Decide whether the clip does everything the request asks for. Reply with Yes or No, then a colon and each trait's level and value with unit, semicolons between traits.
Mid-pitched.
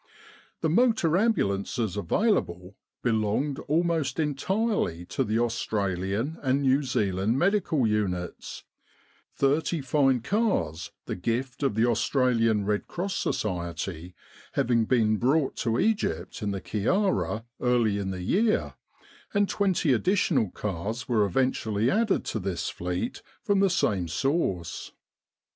No: low, 120 Hz